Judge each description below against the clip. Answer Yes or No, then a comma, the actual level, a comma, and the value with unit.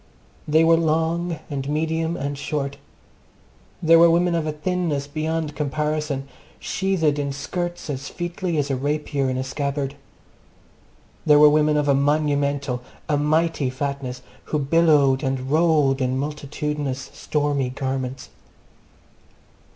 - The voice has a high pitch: No, medium, 150 Hz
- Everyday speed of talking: No, slow, 130 wpm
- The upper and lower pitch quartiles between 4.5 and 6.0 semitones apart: No, narrow, 2.5 semitones